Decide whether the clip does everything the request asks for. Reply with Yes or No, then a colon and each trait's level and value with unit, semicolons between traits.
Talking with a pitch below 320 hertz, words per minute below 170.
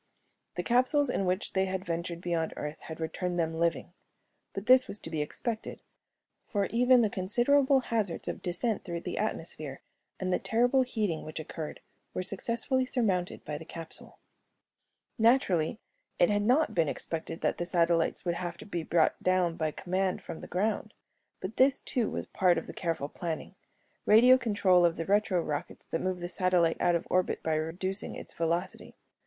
No: medium, 185 Hz; average, 180 wpm